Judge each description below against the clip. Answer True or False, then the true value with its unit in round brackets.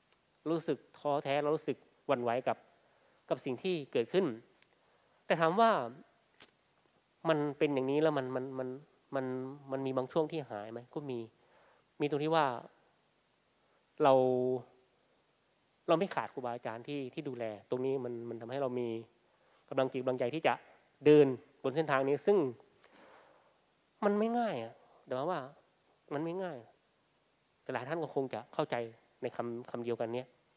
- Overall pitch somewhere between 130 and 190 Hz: True (135 Hz)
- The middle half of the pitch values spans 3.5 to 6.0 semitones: True (3.9 semitones)